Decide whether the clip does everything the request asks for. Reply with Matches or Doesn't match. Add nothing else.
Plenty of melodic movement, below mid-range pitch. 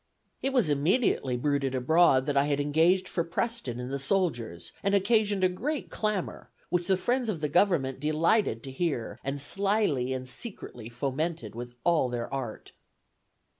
Doesn't match